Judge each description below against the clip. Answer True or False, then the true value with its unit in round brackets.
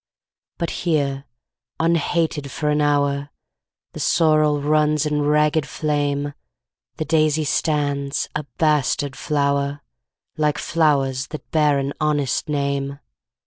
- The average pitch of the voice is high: False (150 Hz)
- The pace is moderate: False (110 wpm)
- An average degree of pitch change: False (1.4 semitones)